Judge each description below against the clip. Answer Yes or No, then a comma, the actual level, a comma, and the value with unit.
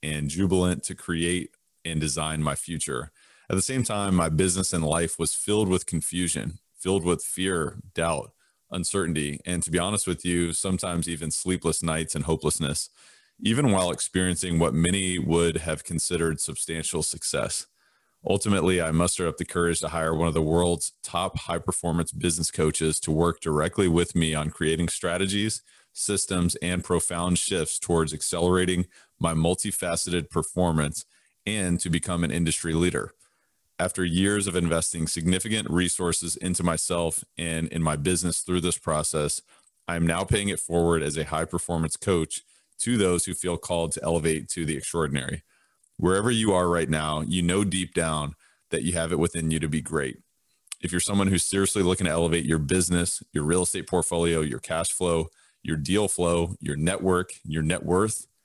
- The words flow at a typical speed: Yes, average, 170 wpm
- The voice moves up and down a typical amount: No, narrow, 2.0 semitones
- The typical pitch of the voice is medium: No, very low, 85 Hz